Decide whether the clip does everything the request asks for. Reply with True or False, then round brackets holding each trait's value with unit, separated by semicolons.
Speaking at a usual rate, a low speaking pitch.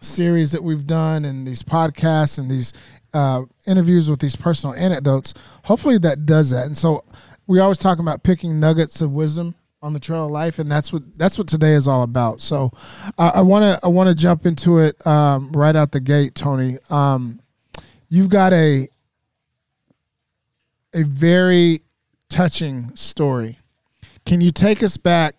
False (175 wpm; 155 Hz)